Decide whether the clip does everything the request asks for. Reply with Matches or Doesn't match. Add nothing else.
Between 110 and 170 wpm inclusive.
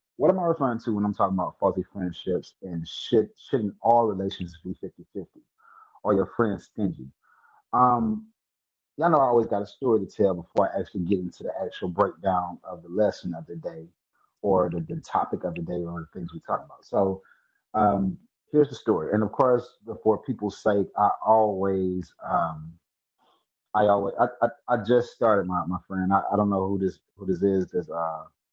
Doesn't match